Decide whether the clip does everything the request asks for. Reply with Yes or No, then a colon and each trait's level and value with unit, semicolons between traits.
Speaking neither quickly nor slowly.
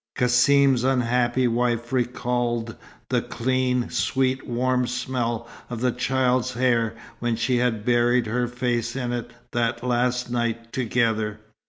No: slow, 130 wpm